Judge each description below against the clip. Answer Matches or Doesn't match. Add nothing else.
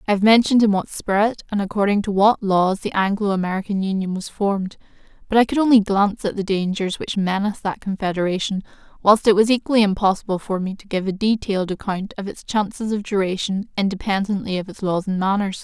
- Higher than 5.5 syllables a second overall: Matches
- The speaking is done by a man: Doesn't match